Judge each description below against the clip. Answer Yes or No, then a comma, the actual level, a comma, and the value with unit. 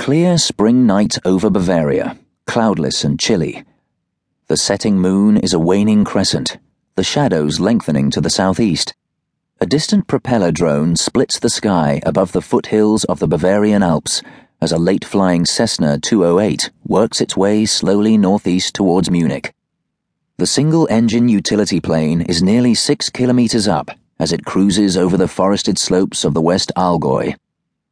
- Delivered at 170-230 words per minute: No, average, 150 wpm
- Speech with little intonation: No, average, 4.4 semitones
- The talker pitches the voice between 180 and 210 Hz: No, low, 100 Hz